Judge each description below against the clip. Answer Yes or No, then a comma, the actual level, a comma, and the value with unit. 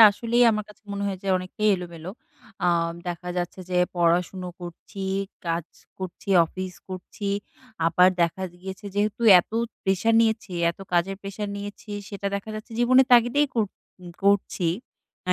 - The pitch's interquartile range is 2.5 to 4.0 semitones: Yes, average, 3.0 semitones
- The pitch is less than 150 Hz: No, high, 195 Hz